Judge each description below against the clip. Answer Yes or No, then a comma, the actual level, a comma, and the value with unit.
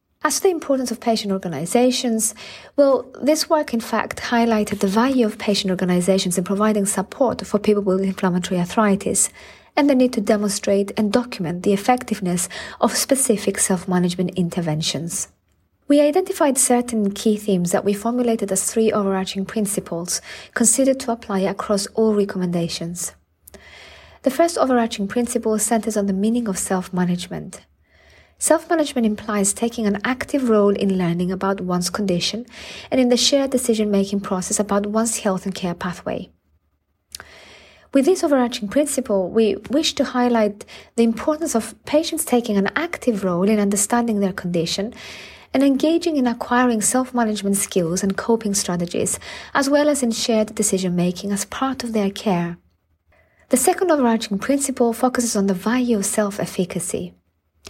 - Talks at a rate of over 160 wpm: No, average, 145 wpm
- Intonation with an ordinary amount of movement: Yes, average, 4.2 semitones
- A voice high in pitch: Yes, high, 215 Hz